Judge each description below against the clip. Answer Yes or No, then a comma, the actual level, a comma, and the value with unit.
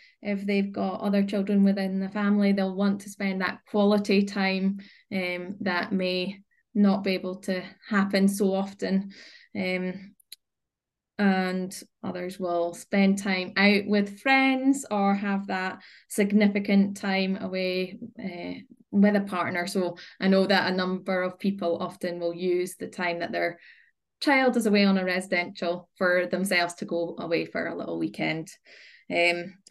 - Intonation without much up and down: Yes, narrow, 1.9 semitones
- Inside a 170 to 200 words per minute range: No, average, 150 wpm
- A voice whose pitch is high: Yes, high, 195 Hz